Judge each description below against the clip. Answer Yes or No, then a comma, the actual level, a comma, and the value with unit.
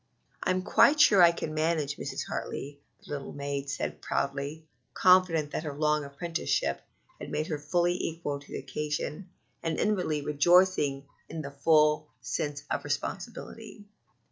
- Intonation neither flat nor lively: Yes, average, 3.1 semitones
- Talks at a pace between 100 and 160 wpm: Yes, average, 145 wpm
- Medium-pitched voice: Yes, medium, 150 Hz